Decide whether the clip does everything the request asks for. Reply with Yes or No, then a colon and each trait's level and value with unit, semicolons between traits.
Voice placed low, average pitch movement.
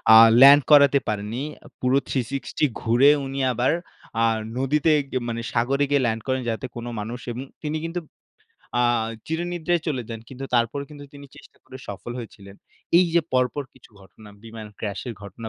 Yes: low, 130 Hz; average, 3.8 semitones